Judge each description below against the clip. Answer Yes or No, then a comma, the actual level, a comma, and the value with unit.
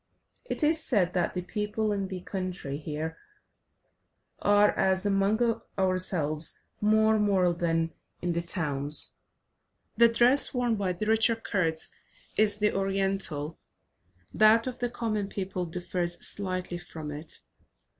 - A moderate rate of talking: No, slow, 130 wpm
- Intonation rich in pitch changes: No, average, 3.8 semitones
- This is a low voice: No, high, 195 Hz